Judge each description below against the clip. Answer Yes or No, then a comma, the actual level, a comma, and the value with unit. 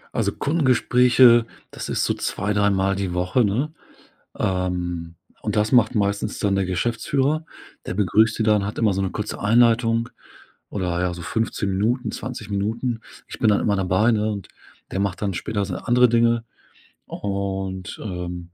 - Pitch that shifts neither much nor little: Yes, average, 3.5 semitones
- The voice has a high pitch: No, low, 105 Hz